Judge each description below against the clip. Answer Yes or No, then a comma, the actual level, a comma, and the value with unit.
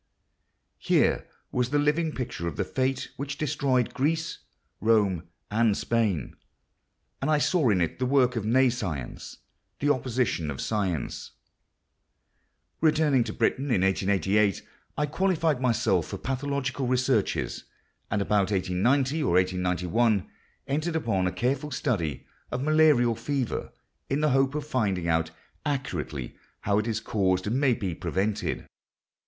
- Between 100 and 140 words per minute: Yes, slow, 135 wpm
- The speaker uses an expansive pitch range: Yes, wide, 6.5 semitones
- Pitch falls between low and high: No, low, 120 Hz